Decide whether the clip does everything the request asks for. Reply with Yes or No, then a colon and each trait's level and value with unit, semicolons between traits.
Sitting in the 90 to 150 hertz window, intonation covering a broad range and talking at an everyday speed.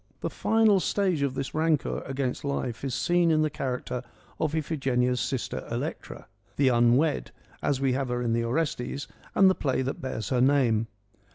No: low, 135 Hz; average, 3.8 semitones; average, 195 wpm